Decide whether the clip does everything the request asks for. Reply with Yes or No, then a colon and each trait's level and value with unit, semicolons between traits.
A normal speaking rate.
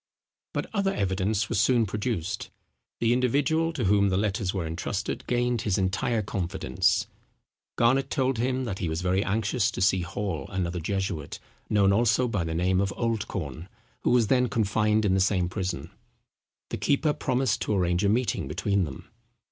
Yes: average, 170 wpm